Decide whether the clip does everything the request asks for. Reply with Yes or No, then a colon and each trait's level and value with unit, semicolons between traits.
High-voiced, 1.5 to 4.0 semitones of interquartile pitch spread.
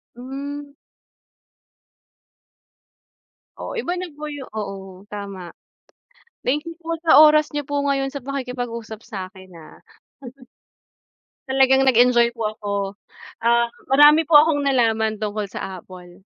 No: very high, 250 Hz; wide, 5.5 semitones